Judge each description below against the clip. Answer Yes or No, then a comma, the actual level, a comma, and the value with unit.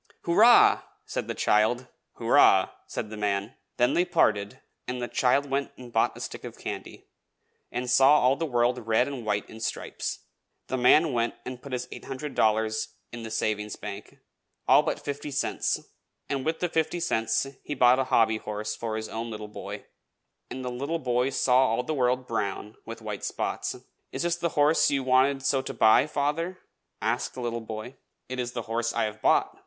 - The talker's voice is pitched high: No, low, 125 Hz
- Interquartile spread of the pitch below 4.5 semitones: Yes, average, 3.7 semitones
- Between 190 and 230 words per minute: Yes, average, 195 wpm